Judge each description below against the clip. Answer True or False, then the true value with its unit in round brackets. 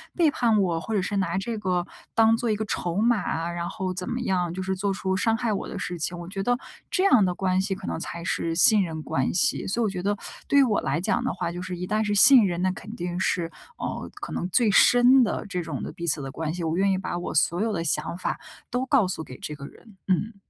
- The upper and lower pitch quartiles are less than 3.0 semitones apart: False (3.9 semitones)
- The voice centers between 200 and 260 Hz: False (190 Hz)